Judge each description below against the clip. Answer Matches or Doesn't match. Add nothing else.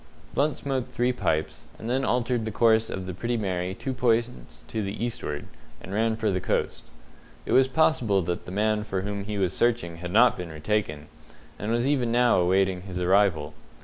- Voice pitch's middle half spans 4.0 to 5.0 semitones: Matches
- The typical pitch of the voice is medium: Doesn't match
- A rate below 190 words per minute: Doesn't match